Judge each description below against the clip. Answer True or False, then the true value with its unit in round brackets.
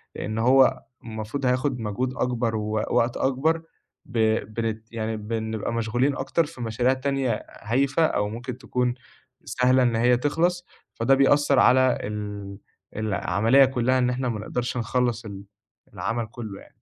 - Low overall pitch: True (120 Hz)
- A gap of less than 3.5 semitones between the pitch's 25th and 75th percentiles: True (2.9 semitones)